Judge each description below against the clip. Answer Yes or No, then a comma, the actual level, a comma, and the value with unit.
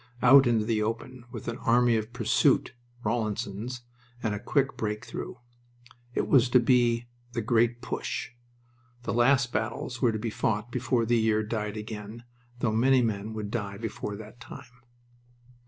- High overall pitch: No, low, 115 Hz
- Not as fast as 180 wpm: Yes, average, 160 wpm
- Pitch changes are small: Yes, narrow, 2.1 semitones